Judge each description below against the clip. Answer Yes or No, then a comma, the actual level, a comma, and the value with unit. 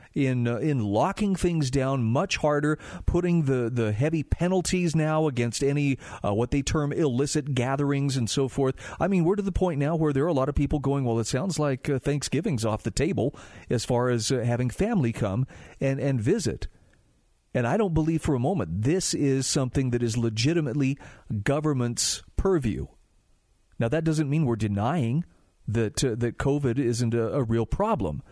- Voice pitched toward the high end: No, low, 135 Hz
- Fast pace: No, average, 190 wpm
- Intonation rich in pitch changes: No, average, 4.3 semitones